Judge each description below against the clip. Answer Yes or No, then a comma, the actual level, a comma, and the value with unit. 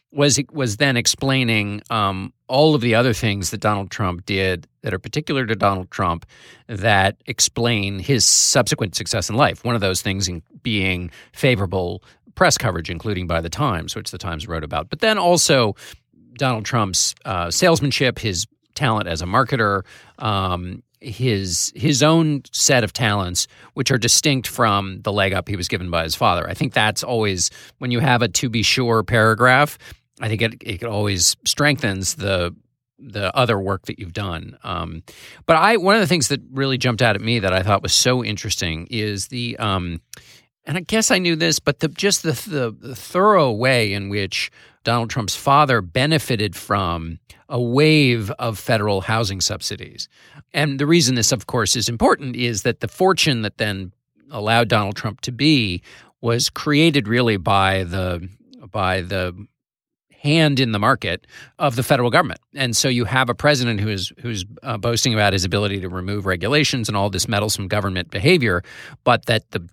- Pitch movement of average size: Yes, average, 5.0 semitones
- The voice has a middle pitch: No, low, 115 Hz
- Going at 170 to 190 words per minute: Yes, average, 180 wpm